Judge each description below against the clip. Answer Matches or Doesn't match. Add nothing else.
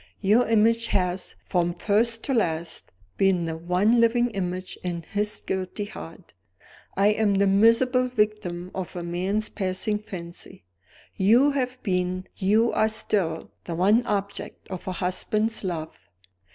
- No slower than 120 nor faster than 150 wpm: Matches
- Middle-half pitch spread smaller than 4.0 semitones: Matches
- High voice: Matches